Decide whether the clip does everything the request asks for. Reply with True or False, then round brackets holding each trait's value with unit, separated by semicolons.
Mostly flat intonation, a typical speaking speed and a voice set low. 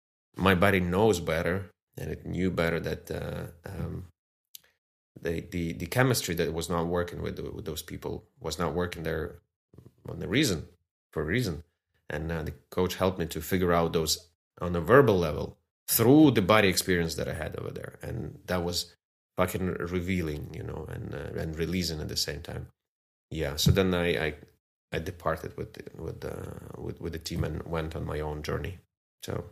False (2.1 semitones; 185 wpm; 85 Hz)